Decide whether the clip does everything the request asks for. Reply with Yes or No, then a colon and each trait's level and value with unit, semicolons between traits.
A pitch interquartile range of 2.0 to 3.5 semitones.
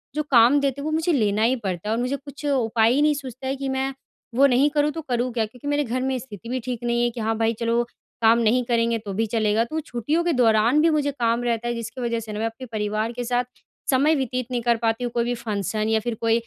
Yes: average, 2.9 semitones